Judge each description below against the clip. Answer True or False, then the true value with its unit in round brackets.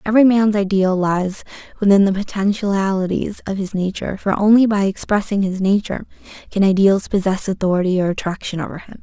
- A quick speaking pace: False (160 wpm)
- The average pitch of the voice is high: True (195 Hz)